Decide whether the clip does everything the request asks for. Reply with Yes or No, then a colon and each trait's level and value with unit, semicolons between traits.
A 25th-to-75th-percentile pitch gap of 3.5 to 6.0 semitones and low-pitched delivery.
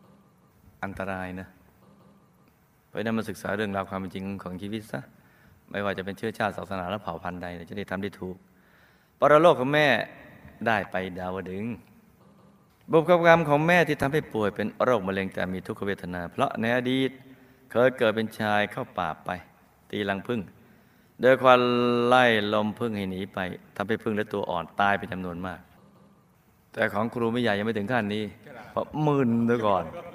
Yes: average, 4.2 semitones; low, 105 Hz